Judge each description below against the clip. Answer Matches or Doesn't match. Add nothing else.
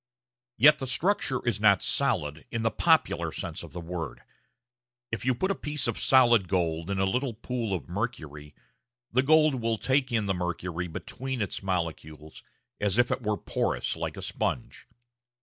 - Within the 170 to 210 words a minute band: Matches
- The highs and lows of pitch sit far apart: Matches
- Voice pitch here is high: Doesn't match